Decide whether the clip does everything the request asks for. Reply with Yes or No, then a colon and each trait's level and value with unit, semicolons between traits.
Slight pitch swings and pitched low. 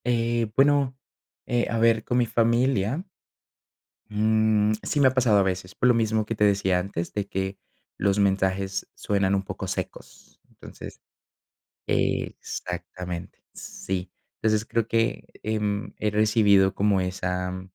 No: average, 3.2 semitones; low, 105 Hz